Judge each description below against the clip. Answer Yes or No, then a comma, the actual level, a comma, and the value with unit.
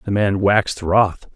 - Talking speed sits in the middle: Yes, average, 175 wpm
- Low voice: Yes, low, 100 Hz